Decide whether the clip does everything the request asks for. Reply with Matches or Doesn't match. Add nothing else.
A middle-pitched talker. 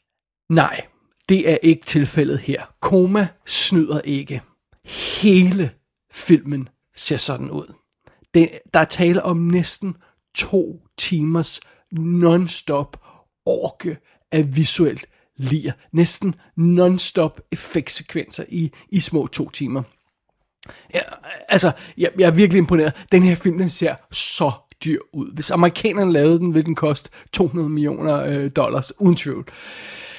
Matches